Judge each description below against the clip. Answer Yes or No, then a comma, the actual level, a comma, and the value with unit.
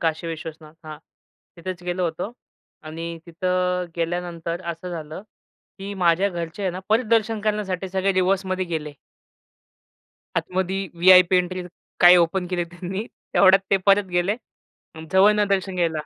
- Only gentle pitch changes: Yes, narrow, 2.2 semitones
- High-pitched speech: No, medium, 180 Hz